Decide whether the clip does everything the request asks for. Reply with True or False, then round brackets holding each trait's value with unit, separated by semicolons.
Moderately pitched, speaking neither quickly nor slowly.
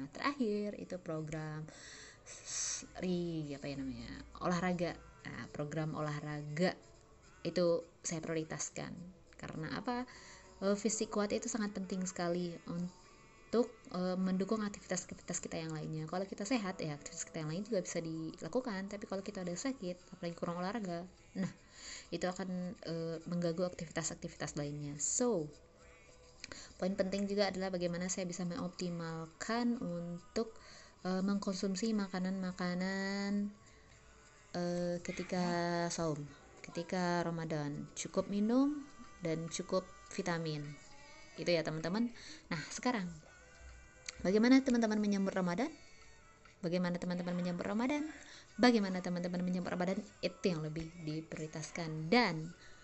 True (180 Hz; 110 wpm)